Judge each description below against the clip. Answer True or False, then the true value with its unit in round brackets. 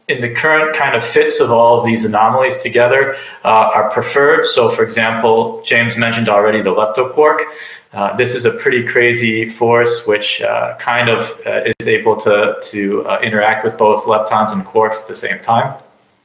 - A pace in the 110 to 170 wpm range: False (185 wpm)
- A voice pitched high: False (130 Hz)